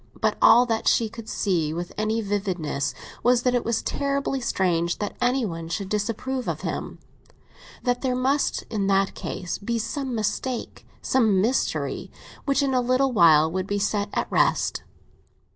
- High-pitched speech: Yes, high, 220 Hz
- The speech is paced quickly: No, average, 160 wpm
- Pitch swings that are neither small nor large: Yes, average, 4.5 semitones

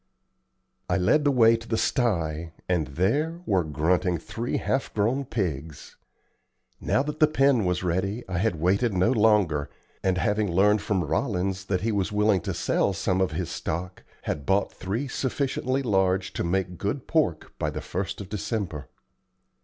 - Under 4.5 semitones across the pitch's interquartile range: Yes, average, 4.1 semitones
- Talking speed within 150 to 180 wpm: Yes, average, 170 wpm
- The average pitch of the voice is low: Yes, very low, 95 Hz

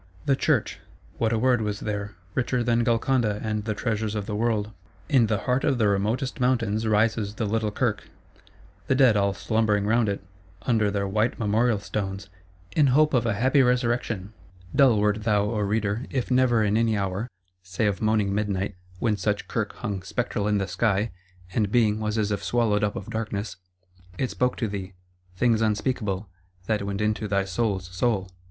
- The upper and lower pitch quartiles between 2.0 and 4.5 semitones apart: Yes, narrow, 2.5 semitones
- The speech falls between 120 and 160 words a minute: No, average, 180 wpm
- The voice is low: Yes, low, 105 Hz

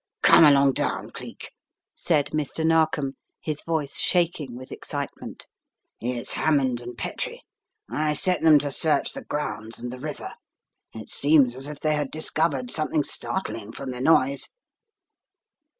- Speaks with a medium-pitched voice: Yes, medium, 145 Hz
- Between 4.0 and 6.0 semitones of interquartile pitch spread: No, average, 3.4 semitones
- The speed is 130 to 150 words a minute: Yes, average, 145 wpm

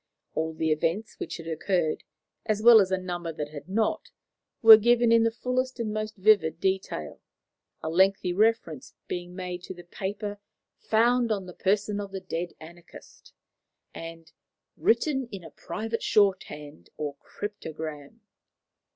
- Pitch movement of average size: Yes, average, 4.7 semitones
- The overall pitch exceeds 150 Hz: Yes, high, 190 Hz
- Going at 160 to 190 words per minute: No, average, 150 wpm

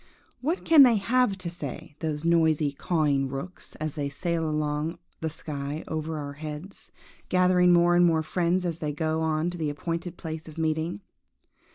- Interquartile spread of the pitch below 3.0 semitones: Yes, narrow, 2.5 semitones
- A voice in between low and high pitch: Yes, medium, 160 Hz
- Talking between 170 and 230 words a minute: Yes, average, 180 wpm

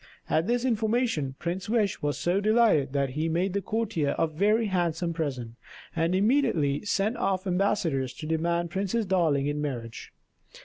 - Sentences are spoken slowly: No, average, 160 wpm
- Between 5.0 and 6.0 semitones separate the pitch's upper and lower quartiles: Yes, wide, 5.6 semitones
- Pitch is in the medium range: Yes, medium, 175 Hz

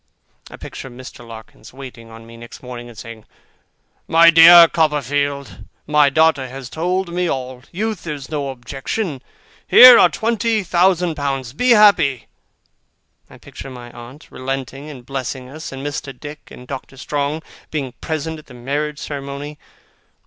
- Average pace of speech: Yes, average, 150 wpm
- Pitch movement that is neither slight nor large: Yes, average, 3.9 semitones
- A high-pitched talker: No, medium, 140 Hz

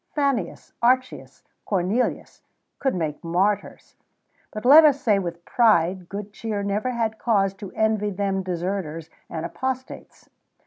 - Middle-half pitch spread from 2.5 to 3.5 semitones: No, average, 4.5 semitones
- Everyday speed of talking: No, slow, 130 wpm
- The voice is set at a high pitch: Yes, high, 205 Hz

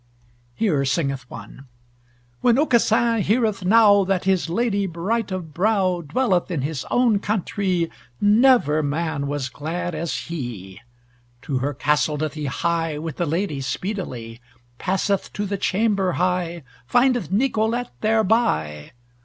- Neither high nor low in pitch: Yes, medium, 180 Hz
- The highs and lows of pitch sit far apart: Yes, wide, 6.1 semitones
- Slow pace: Yes, slow, 130 wpm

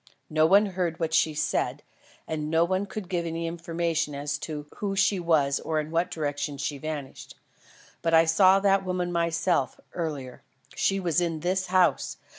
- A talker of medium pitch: Yes, medium, 165 Hz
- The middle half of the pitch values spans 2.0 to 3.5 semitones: Yes, average, 2.7 semitones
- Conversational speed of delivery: Yes, average, 175 wpm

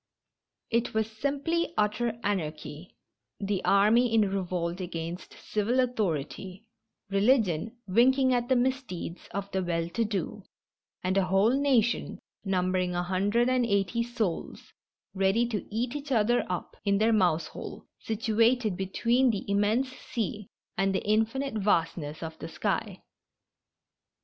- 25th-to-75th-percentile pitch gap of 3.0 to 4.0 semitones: No, average, 4.4 semitones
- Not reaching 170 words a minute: Yes, slow, 135 wpm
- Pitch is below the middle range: No, high, 210 Hz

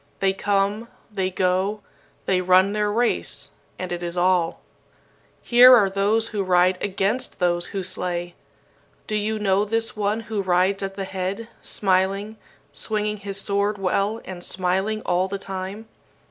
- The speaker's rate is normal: Yes, average, 150 wpm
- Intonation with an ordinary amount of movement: No, narrow, 2.2 semitones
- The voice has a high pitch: Yes, high, 195 Hz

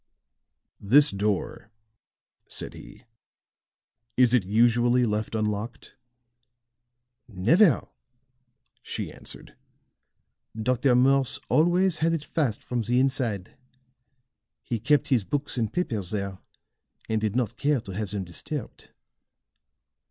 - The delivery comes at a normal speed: No, slow, 105 wpm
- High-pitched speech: No, low, 120 Hz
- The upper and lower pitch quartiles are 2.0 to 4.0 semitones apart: No, average, 4.5 semitones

